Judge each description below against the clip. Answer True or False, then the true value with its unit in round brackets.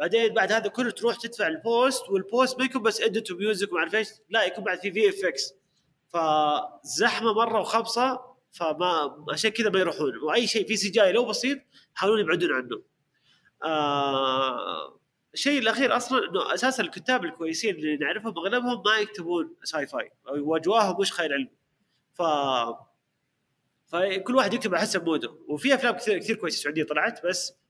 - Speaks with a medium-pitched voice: False (215 Hz)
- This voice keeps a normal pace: False (160 wpm)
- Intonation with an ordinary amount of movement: False (5.9 semitones)